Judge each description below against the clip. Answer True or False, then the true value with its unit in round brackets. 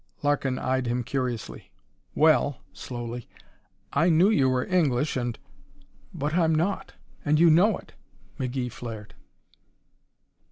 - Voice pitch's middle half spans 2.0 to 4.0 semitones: False (4.4 semitones)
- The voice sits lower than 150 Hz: True (135 Hz)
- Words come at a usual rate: False (125 wpm)